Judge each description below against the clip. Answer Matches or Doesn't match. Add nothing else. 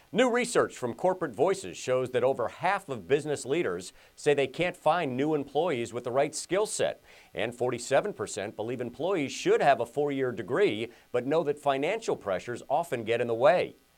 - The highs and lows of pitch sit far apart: Doesn't match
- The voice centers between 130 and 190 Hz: Matches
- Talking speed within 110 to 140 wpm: Doesn't match